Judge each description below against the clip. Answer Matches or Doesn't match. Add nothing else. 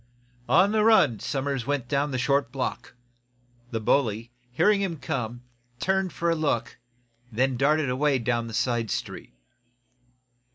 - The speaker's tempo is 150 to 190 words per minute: Doesn't match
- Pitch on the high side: Doesn't match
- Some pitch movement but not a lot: Matches